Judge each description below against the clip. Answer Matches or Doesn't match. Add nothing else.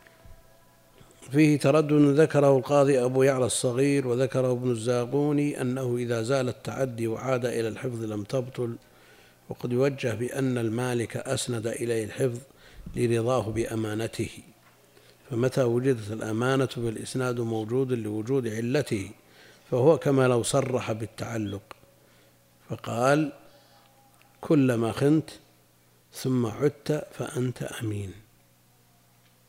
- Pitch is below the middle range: Matches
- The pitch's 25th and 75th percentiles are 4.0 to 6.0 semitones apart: Doesn't match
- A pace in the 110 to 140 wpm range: Doesn't match